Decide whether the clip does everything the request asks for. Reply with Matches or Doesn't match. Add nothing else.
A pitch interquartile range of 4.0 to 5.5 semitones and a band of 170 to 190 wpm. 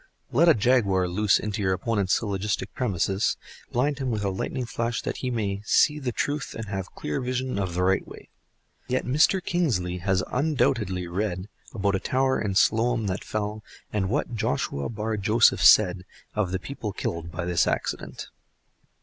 Matches